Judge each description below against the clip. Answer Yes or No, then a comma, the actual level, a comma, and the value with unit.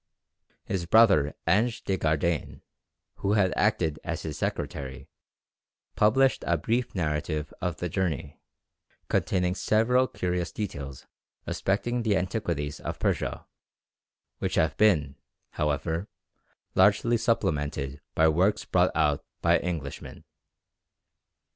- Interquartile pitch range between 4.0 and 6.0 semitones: Yes, wide, 5.6 semitones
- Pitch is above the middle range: No, very low, 90 Hz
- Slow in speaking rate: Yes, slow, 110 wpm